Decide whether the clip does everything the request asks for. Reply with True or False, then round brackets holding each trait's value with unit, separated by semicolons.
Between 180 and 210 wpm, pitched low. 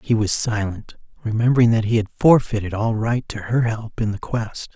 True (200 wpm; 110 Hz)